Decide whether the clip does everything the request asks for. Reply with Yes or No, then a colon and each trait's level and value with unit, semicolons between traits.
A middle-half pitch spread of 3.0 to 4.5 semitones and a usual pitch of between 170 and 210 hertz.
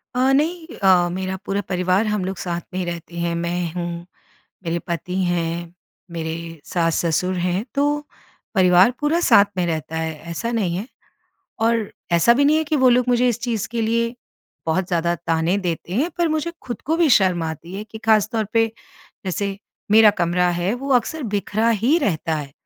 No: wide, 5.5 semitones; high, 190 Hz